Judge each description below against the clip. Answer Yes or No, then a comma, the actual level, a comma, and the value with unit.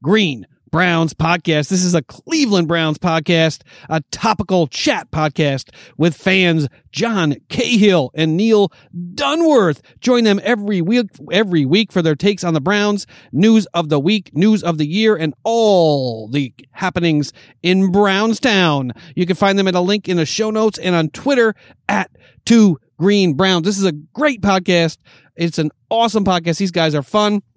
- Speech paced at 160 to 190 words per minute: Yes, average, 170 wpm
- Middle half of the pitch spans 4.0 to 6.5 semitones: Yes, average, 4.6 semitones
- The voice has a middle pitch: Yes, medium, 180 Hz